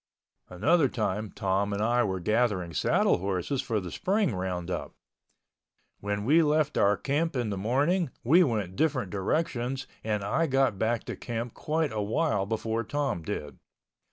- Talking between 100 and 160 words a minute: Yes, average, 155 wpm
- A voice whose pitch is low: Yes, low, 110 Hz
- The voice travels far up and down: Yes, wide, 6.1 semitones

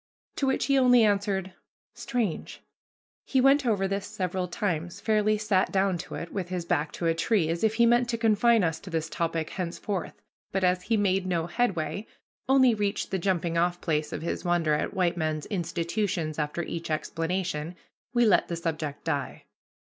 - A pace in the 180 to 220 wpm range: Yes, average, 185 wpm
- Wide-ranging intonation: No, average, 4.3 semitones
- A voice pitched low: No, medium, 185 Hz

